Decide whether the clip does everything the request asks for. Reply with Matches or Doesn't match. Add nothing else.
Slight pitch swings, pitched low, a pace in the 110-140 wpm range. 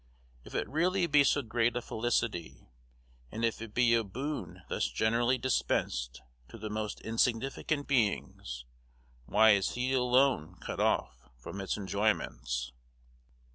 Doesn't match